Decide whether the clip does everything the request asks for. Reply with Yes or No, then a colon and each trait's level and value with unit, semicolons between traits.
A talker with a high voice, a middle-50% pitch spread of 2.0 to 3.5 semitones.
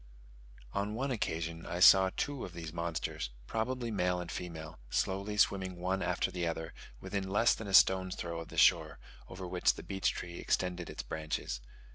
No: very low, 90 Hz; average, 2.8 semitones